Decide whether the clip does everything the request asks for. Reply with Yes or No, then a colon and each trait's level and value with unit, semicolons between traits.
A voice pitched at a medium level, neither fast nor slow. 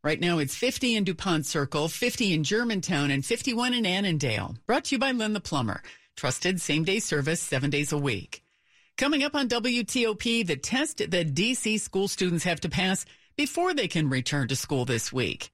Yes: medium, 180 Hz; average, 195 wpm